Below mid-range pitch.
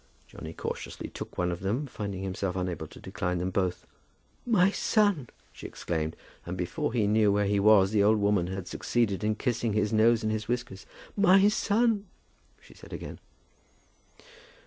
Yes: low, 105 Hz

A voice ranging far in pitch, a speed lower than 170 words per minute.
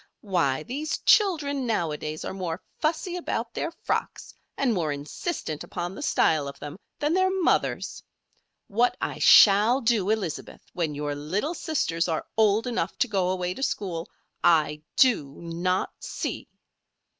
Yes: wide, 8.1 semitones; average, 145 wpm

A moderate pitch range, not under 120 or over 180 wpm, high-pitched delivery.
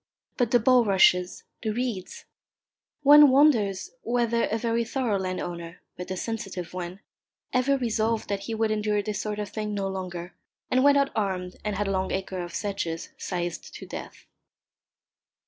Yes: average, 3.9 semitones; average, 165 wpm; high, 210 Hz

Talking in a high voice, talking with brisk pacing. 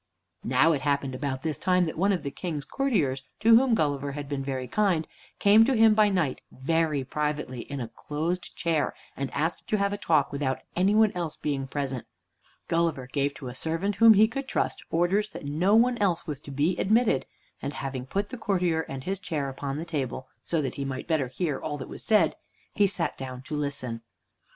No: medium, 155 Hz; fast, 210 wpm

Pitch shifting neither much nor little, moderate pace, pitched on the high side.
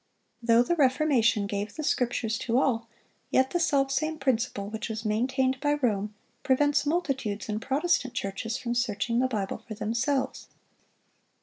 Yes: average, 3.7 semitones; average, 145 wpm; high, 245 Hz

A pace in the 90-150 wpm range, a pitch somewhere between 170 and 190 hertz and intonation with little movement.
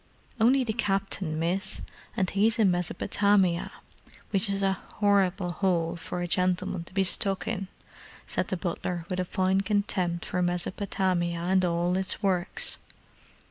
Yes: average, 145 wpm; medium, 185 Hz; narrow, 1.9 semitones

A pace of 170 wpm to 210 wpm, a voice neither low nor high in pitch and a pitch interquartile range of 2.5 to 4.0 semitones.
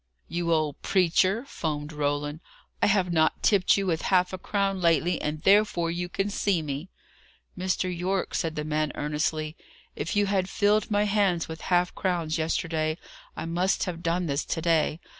Yes: average, 175 wpm; medium, 170 Hz; average, 3.3 semitones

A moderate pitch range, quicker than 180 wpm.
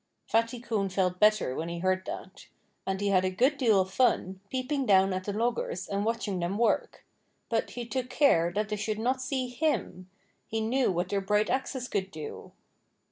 Yes: average, 4.5 semitones; average, 195 wpm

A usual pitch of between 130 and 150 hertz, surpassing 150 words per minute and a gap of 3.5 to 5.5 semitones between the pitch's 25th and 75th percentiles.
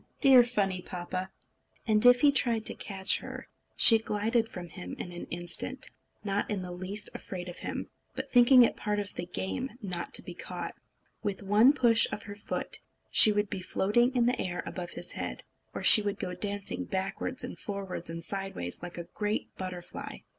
No: high, 205 Hz; average, 190 wpm; average, 3.8 semitones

